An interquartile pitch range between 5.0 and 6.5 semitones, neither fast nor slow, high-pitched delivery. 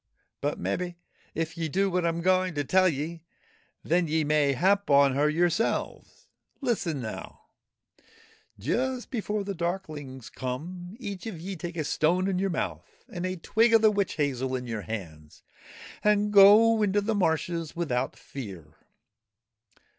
No: wide, 5.4 semitones; average, 160 wpm; medium, 170 Hz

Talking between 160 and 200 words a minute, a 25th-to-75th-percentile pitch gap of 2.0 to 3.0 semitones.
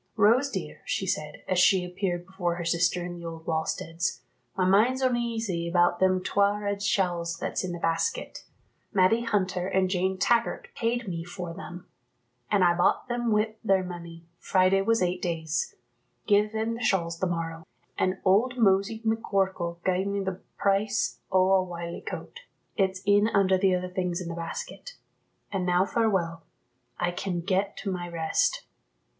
Yes: average, 170 wpm; average, 2.7 semitones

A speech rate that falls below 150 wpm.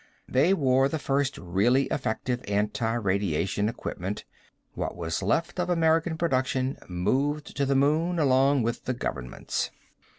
Yes: slow, 135 wpm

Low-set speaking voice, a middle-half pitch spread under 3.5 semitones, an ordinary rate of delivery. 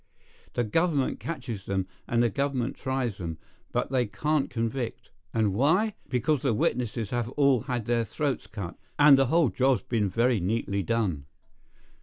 No: low, 120 Hz; average, 3.8 semitones; average, 155 wpm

